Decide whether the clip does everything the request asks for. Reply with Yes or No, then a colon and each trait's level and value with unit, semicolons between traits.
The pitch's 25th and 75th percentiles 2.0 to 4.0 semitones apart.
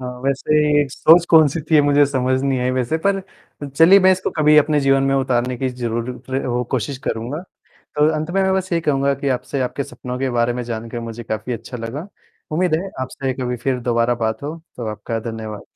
Yes: average, 3.7 semitones